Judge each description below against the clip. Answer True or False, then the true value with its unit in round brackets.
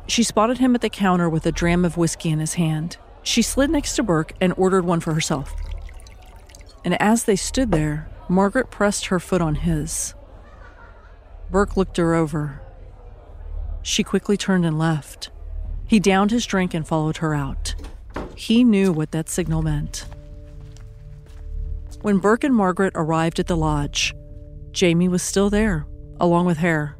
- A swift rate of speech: False (160 wpm)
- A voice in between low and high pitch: True (165 Hz)